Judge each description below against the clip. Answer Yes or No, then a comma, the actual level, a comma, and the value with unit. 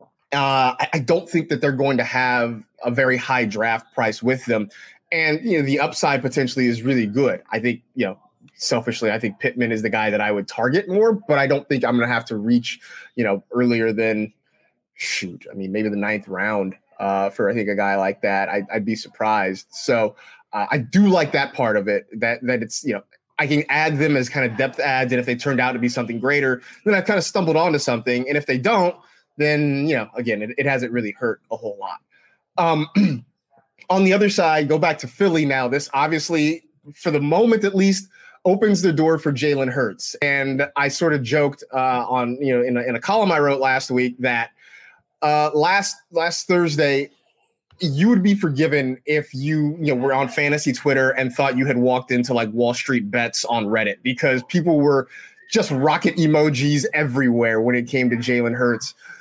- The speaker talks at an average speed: No, fast, 215 wpm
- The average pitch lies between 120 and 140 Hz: Yes, low, 135 Hz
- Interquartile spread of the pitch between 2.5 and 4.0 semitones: No, average, 4.4 semitones